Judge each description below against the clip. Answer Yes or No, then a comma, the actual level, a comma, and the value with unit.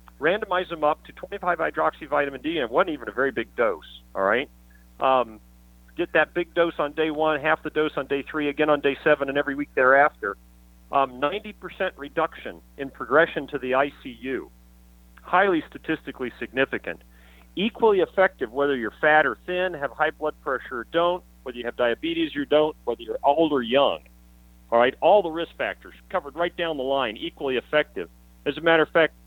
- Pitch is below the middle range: No, medium, 145 Hz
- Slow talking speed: No, average, 190 wpm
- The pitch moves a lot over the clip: Yes, wide, 5.9 semitones